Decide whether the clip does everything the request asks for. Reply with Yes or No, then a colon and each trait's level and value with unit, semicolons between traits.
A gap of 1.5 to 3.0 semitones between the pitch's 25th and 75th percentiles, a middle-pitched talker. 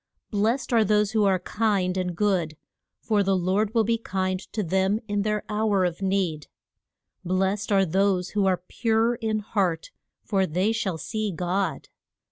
No: narrow, 2.5 semitones; high, 195 Hz